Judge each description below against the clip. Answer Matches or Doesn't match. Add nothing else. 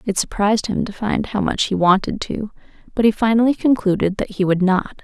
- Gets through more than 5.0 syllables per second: Matches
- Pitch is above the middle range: Matches